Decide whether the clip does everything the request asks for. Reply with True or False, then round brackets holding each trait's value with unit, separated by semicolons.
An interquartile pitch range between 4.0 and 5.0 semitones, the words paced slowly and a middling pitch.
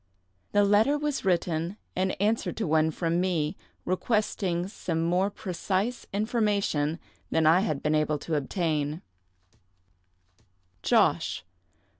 True (4.3 semitones; 115 wpm; 180 Hz)